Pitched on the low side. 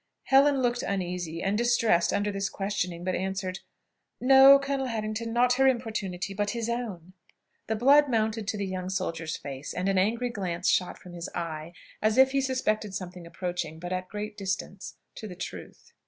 No: high, 200 Hz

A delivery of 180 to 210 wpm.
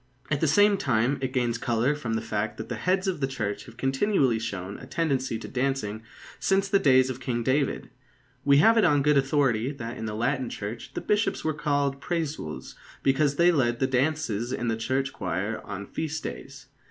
Yes: average, 200 wpm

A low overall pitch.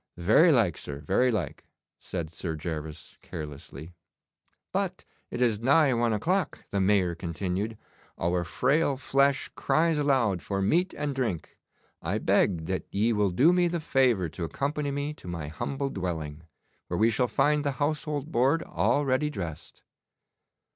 Yes: low, 115 Hz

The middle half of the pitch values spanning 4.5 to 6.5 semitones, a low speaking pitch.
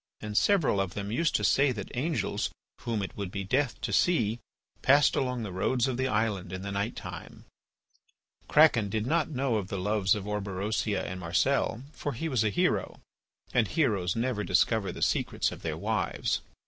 Yes: average, 4.8 semitones; low, 110 Hz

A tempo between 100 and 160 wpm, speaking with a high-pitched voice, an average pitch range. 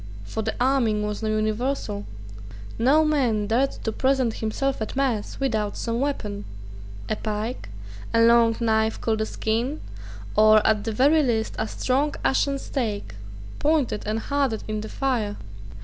Yes: average, 150 wpm; high, 225 Hz; average, 3.8 semitones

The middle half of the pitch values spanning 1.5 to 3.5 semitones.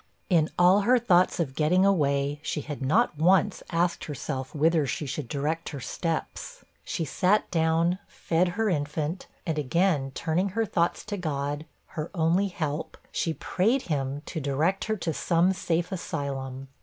No: average, 3.9 semitones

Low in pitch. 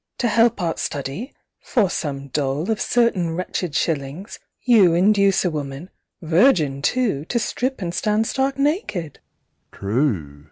No: medium, 185 Hz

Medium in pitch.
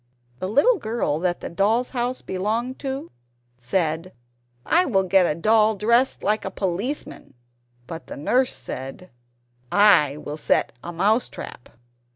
No: high, 200 Hz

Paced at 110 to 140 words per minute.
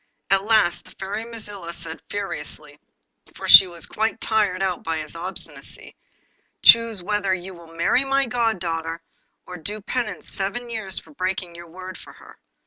No: average, 160 wpm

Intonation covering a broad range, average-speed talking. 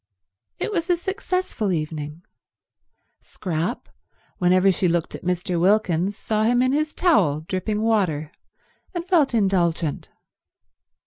No: wide, 6.4 semitones; slow, 120 wpm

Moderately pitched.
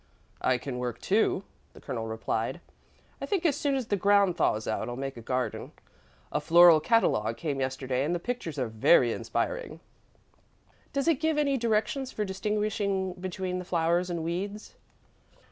Yes: medium, 180 Hz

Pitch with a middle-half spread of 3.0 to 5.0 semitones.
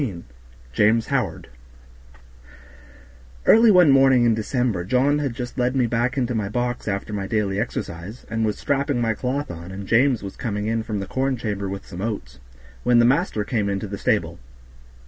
Yes: average, 4.2 semitones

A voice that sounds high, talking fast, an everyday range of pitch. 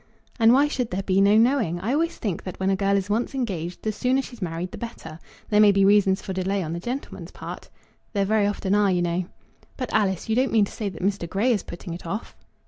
Yes: high, 200 Hz; fast, 250 wpm; average, 3.5 semitones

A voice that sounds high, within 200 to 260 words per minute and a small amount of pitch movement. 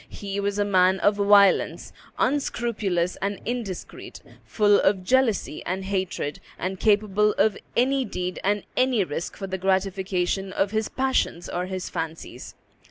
No: high, 200 Hz; average, 145 wpm; narrow, 2.2 semitones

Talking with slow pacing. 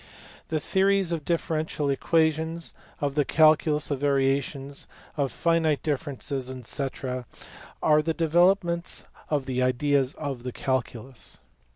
Yes: slow, 125 wpm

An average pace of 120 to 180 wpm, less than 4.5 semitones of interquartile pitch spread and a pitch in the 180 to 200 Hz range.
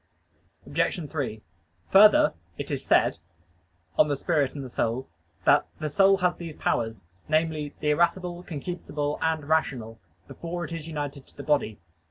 No: average, 145 wpm; average, 3.3 semitones; medium, 150 Hz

